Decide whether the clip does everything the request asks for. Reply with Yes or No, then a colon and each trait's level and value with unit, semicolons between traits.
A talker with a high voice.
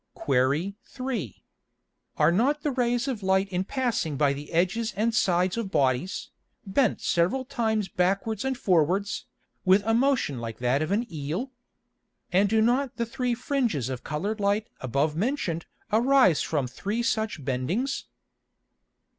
Yes: high, 200 Hz